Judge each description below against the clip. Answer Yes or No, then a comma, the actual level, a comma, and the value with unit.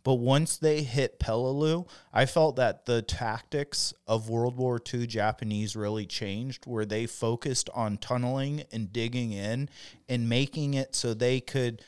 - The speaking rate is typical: Yes, average, 155 wpm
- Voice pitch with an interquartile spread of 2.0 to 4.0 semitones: Yes, average, 3.1 semitones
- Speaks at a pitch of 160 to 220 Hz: No, low, 125 Hz